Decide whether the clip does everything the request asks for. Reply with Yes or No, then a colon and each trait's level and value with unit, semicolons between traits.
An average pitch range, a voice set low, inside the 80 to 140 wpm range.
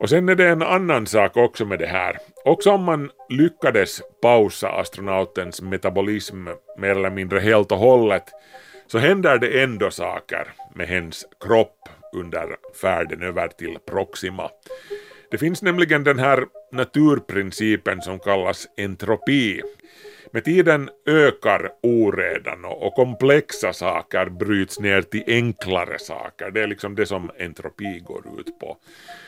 No: wide, 8.9 semitones; low, 125 Hz; average, 135 wpm